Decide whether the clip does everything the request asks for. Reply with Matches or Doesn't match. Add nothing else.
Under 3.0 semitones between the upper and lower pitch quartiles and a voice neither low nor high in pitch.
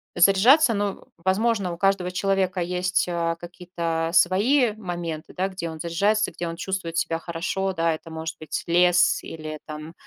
Matches